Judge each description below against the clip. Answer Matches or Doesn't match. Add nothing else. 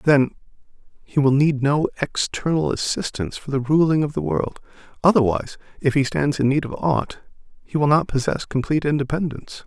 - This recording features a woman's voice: Doesn't match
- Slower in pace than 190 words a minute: Matches